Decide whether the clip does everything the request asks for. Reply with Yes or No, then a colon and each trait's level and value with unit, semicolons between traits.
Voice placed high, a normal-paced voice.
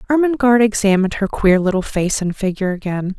Yes: high, 205 Hz; average, 170 wpm